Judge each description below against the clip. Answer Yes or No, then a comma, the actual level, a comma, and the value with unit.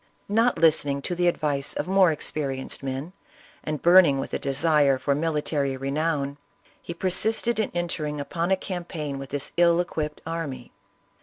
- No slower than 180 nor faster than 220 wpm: No, average, 160 wpm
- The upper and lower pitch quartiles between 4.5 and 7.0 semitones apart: No, average, 3.8 semitones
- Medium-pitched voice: Yes, medium, 155 Hz